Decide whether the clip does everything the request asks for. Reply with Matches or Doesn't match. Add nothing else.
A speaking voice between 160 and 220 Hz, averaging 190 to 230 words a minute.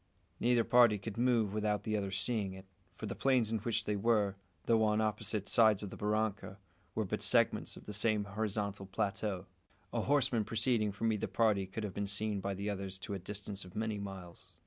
Doesn't match